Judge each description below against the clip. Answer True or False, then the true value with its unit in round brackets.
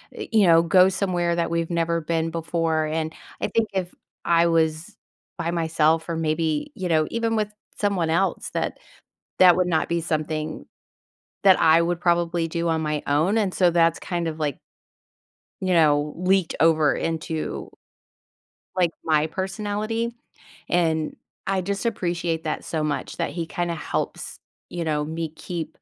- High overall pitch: False (170 Hz)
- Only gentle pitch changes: True (2.3 semitones)